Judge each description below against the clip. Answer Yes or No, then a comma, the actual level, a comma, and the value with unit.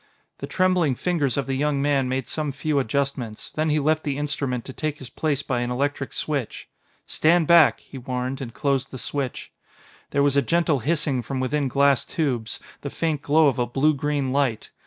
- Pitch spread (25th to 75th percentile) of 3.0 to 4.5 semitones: No, narrow, 2.5 semitones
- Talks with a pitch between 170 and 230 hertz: No, medium, 140 Hz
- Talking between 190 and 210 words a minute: Yes, average, 200 wpm